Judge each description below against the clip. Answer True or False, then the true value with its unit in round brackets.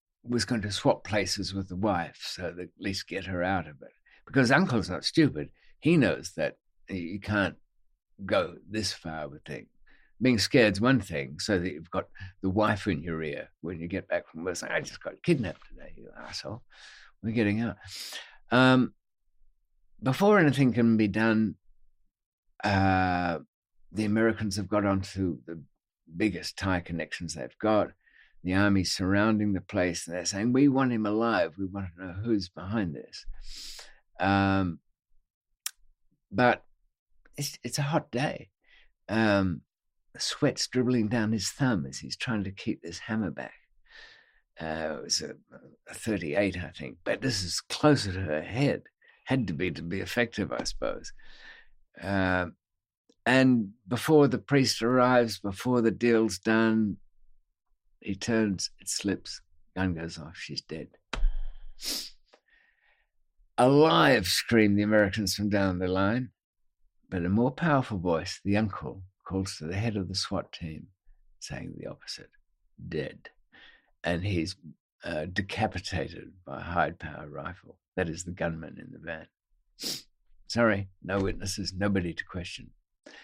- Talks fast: False (150 wpm)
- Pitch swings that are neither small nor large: True (3.6 semitones)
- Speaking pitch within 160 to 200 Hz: False (100 Hz)